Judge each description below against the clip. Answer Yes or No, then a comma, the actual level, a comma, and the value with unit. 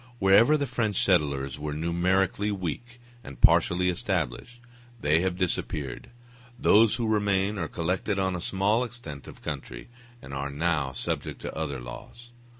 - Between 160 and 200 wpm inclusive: No, average, 150 wpm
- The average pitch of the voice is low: Yes, very low, 90 Hz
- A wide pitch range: Yes, wide, 5.8 semitones